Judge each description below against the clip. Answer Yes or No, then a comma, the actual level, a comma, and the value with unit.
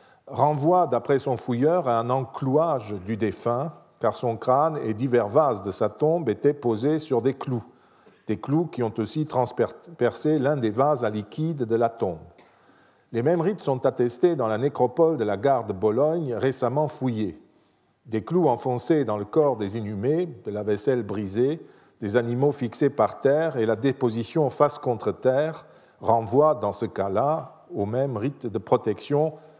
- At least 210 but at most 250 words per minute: No, average, 170 wpm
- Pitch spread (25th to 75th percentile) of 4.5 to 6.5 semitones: Yes, average, 4.8 semitones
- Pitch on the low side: Yes, low, 125 Hz